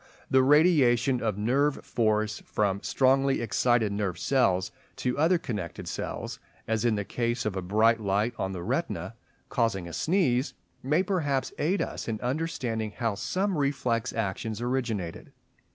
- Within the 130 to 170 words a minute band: Yes, average, 150 wpm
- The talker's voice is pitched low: Yes, low, 120 Hz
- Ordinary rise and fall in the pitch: Yes, average, 4.5 semitones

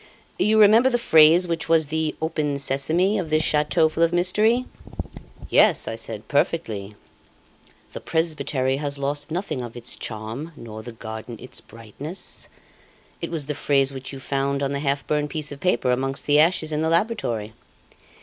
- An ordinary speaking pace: Yes, average, 170 wpm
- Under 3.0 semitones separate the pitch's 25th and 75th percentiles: No, average, 3.8 semitones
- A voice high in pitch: No, medium, 150 Hz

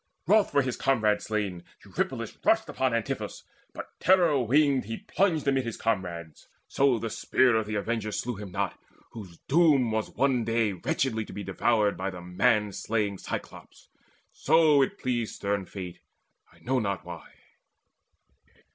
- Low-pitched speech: Yes, low, 115 Hz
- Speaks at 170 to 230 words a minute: No, average, 155 wpm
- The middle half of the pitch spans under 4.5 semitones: No, average, 4.8 semitones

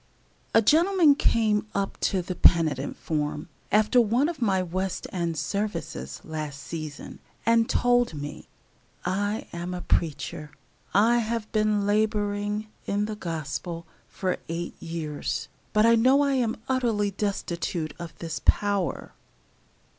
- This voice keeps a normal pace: No, slow, 130 wpm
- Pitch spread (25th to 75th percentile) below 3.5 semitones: No, average, 4.8 semitones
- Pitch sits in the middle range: No, high, 200 Hz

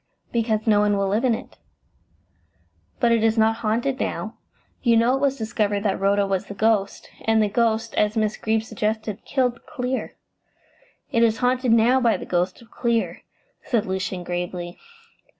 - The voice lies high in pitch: Yes, high, 220 Hz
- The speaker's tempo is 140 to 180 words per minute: Yes, average, 170 wpm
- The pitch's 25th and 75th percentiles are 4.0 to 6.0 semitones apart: No, narrow, 2.4 semitones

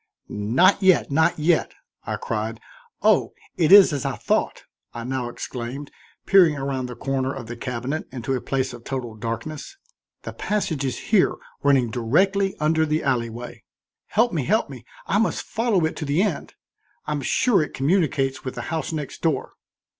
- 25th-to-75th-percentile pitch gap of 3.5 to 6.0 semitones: Yes, average, 4.9 semitones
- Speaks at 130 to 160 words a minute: No, average, 175 wpm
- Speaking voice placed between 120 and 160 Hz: Yes, medium, 140 Hz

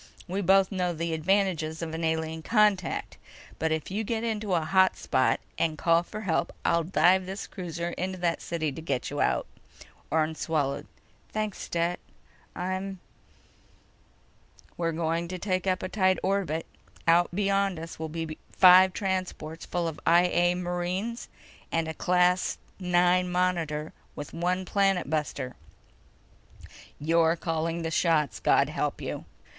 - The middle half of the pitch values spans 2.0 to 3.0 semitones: Yes, narrow, 2.5 semitones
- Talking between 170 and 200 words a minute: No, average, 150 wpm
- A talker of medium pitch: Yes, medium, 175 Hz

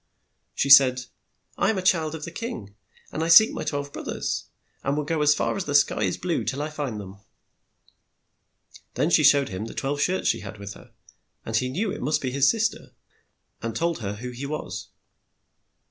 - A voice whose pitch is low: No, medium, 145 Hz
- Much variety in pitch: No, average, 4.7 semitones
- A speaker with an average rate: No, fast, 210 wpm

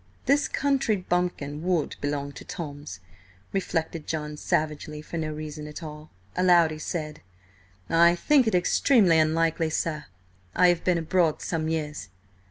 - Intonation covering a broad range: No, average, 2.8 semitones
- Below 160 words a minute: Yes, average, 145 wpm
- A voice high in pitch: No, medium, 160 Hz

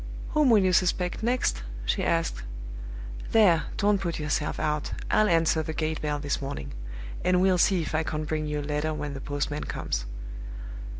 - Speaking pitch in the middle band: Yes, medium, 155 Hz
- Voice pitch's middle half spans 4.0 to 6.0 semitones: No, average, 3.6 semitones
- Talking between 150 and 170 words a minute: No, average, 180 wpm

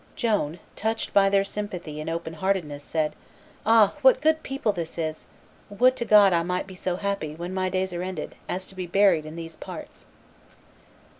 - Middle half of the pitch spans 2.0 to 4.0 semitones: Yes, average, 3.7 semitones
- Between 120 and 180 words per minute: No, average, 195 wpm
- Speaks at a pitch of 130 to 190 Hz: Yes, medium, 185 Hz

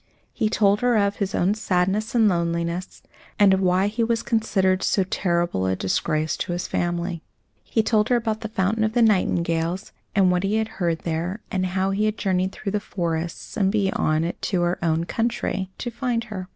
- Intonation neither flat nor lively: Yes, average, 3.7 semitones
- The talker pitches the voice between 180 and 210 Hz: Yes, high, 190 Hz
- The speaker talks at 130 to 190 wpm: No, average, 200 wpm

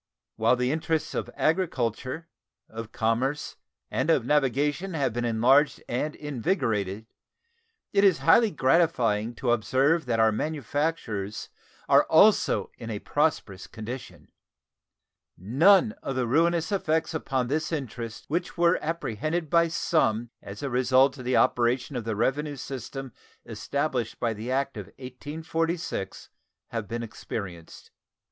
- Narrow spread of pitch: No, wide, 5.6 semitones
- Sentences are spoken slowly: Yes, slow, 130 wpm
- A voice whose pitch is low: Yes, low, 130 Hz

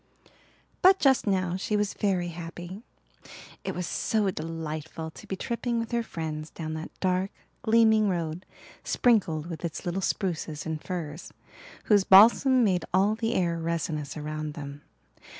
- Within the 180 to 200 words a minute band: No, average, 150 wpm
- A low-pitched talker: No, medium, 180 Hz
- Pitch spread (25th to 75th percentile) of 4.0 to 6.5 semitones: Yes, average, 4.7 semitones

